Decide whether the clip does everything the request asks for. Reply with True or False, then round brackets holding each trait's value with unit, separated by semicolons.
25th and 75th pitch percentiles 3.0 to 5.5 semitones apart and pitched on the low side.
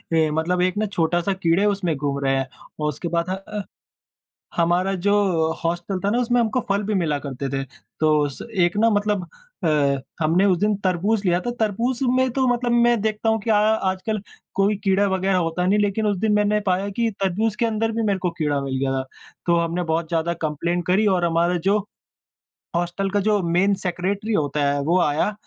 False (3.9 semitones; 185 Hz)